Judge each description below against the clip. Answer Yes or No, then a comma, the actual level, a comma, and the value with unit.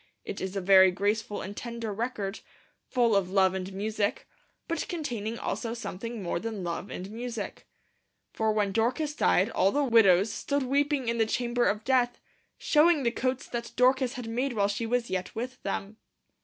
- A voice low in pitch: No, high, 225 Hz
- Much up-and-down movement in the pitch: No, average, 3.8 semitones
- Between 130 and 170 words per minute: No, average, 180 wpm